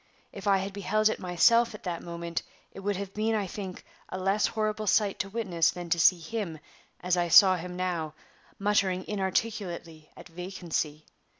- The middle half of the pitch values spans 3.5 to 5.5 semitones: No, average, 3.1 semitones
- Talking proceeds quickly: No, average, 180 wpm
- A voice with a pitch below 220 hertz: Yes, high, 190 Hz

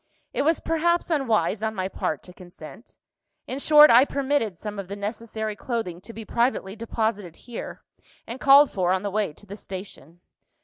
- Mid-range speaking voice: No, high, 220 Hz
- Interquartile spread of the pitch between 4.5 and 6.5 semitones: Yes, average, 5.2 semitones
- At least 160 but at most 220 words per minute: Yes, average, 180 wpm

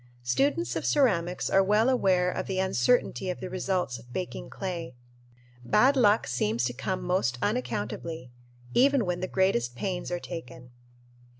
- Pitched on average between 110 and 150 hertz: No, medium, 180 Hz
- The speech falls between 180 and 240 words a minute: No, average, 155 wpm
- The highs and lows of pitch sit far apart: Yes, wide, 7.9 semitones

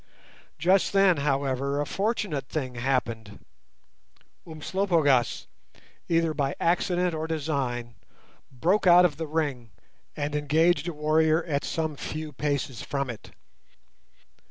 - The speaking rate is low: Yes, slow, 115 wpm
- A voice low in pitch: No, medium, 150 Hz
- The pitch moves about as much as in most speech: Yes, average, 3.3 semitones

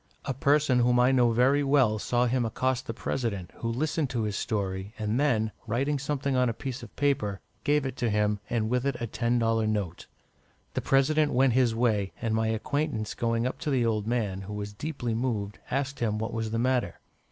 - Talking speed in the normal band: No, fast, 210 wpm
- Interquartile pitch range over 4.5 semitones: No, average, 3.5 semitones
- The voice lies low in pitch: Yes, low, 120 Hz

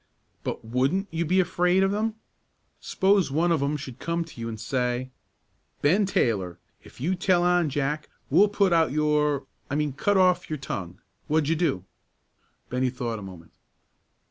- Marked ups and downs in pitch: Yes, wide, 5.8 semitones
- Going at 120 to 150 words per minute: No, average, 170 wpm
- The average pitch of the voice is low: No, medium, 150 Hz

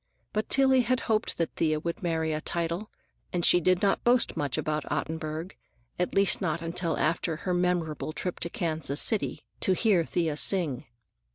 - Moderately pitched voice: Yes, medium, 170 Hz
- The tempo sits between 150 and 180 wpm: Yes, average, 170 wpm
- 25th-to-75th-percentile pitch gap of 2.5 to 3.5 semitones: Yes, average, 3.2 semitones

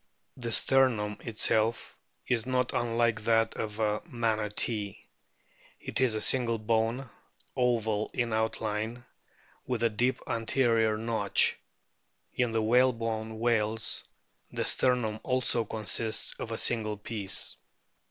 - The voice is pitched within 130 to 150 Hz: No, low, 115 Hz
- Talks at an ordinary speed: No, slow, 115 wpm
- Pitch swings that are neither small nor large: No, narrow, 1.7 semitones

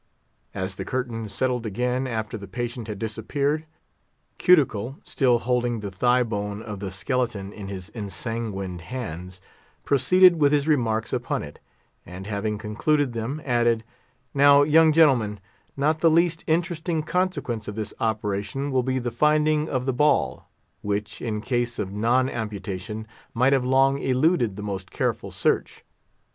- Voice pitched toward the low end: Yes, low, 120 Hz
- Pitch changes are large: No, average, 5.0 semitones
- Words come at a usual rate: Yes, average, 150 wpm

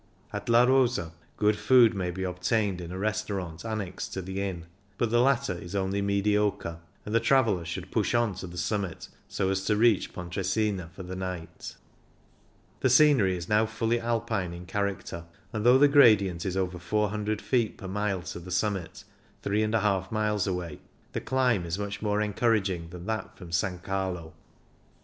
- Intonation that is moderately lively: Yes, average, 3.2 semitones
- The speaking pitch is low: Yes, low, 100 Hz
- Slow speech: No, average, 175 wpm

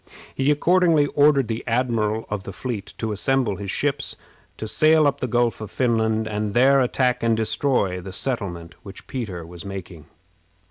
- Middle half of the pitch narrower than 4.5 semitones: No, average, 4.8 semitones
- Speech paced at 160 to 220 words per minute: Yes, average, 170 wpm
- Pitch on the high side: No, low, 115 Hz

